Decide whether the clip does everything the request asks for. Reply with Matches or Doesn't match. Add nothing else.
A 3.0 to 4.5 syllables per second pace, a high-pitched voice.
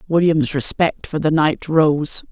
Doesn't match